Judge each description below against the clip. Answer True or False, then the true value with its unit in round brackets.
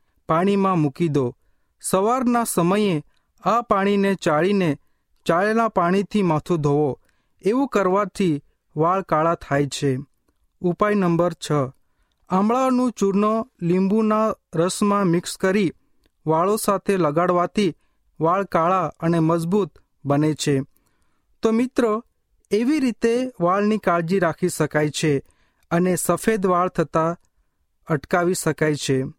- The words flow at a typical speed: False (105 wpm)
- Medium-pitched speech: True (175 Hz)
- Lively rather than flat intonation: False (4.8 semitones)